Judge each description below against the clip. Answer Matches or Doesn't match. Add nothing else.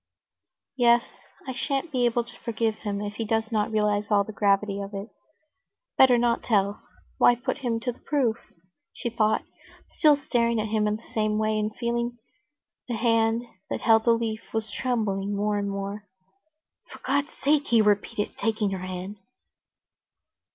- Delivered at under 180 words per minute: Matches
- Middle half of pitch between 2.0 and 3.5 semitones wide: Matches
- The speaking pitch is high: Matches